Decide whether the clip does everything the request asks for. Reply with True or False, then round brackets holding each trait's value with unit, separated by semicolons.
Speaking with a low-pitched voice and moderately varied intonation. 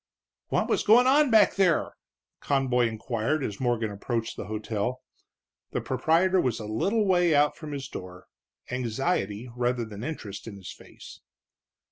False (125 Hz; 6.9 semitones)